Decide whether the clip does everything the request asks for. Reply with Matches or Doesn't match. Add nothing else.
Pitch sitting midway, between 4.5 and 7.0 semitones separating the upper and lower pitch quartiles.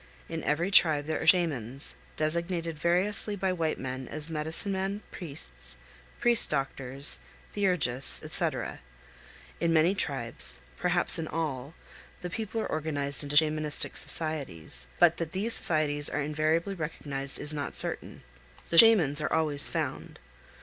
Doesn't match